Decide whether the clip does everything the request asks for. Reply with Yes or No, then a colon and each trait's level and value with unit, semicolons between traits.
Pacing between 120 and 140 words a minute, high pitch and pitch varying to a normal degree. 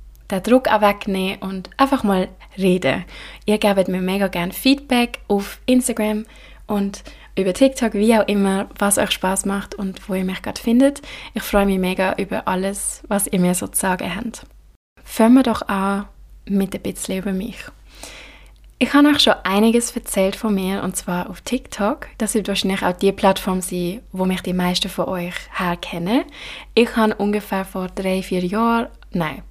No: average, 175 wpm; high, 200 Hz; average, 3.2 semitones